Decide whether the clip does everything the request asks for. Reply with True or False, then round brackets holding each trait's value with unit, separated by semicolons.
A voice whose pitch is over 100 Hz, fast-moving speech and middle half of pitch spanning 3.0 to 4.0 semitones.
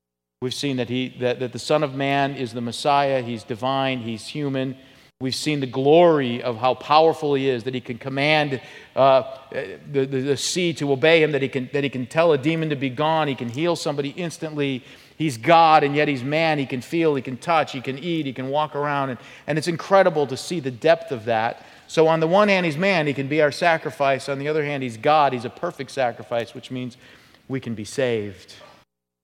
True (140 Hz; 230 wpm; 3.4 semitones)